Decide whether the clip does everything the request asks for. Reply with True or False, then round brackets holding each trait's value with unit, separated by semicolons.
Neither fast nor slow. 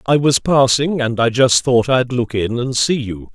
False (235 wpm)